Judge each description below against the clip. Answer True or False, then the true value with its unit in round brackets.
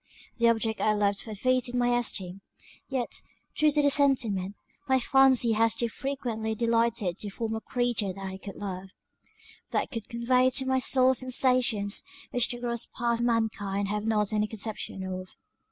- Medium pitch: False (230 Hz)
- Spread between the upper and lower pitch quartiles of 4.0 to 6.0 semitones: False (3.4 semitones)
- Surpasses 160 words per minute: True (170 wpm)